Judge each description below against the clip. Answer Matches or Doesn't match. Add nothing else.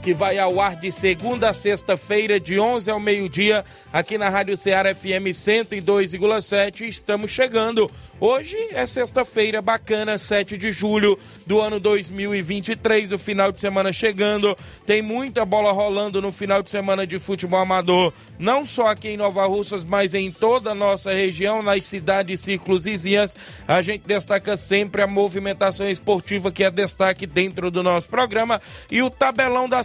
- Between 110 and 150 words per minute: Doesn't match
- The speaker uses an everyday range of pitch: Doesn't match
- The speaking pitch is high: Matches